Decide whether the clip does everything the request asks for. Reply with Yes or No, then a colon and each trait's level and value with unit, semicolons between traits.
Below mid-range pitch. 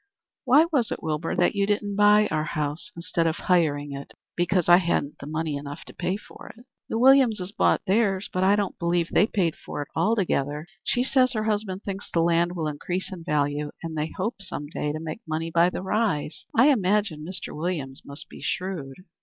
No: medium, 175 Hz